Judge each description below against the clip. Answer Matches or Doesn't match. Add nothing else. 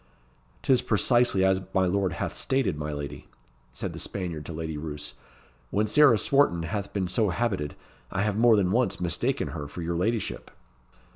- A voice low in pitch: Matches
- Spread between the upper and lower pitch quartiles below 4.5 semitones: Doesn't match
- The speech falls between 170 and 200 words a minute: Matches